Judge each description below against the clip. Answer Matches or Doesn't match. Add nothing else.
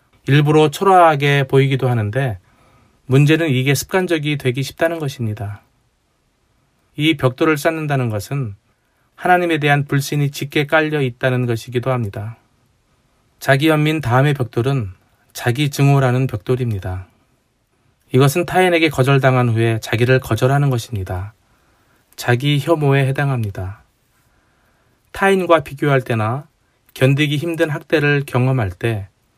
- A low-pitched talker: Matches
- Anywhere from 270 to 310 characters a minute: Matches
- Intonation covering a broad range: Doesn't match